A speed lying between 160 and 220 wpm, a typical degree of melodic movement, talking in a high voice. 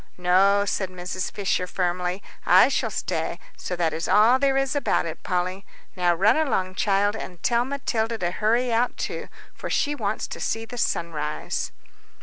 Yes: average, 170 wpm; average, 4.7 semitones; high, 200 Hz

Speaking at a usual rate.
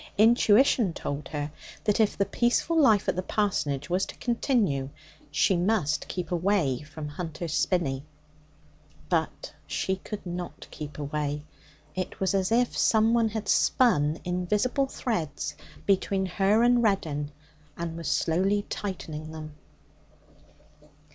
No: slow, 130 wpm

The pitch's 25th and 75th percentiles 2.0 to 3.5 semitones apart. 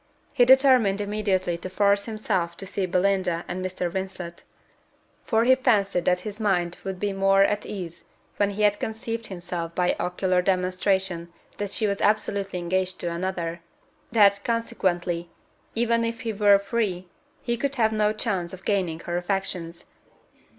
Yes: average, 3.0 semitones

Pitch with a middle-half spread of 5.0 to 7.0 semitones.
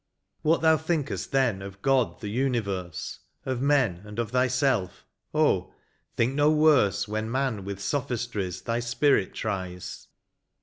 Yes: wide, 5.4 semitones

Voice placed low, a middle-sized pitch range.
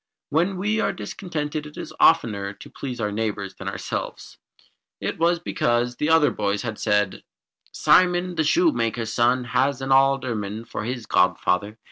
No: low, 125 Hz; wide, 7.1 semitones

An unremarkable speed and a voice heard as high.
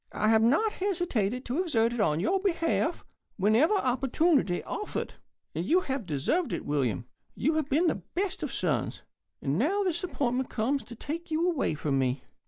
Yes: average, 175 wpm; very high, 270 Hz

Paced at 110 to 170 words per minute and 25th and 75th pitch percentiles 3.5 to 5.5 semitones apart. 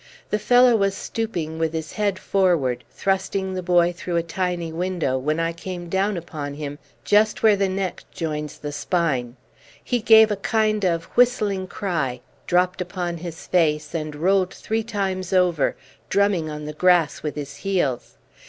Yes: average, 165 wpm; average, 4.0 semitones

